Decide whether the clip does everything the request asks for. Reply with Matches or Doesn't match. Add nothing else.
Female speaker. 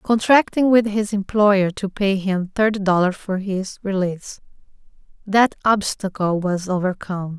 Matches